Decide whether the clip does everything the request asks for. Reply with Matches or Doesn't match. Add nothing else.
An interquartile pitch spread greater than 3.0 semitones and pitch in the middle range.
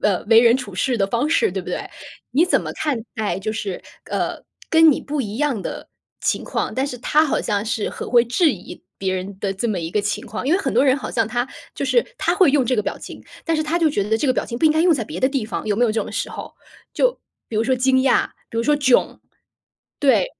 Doesn't match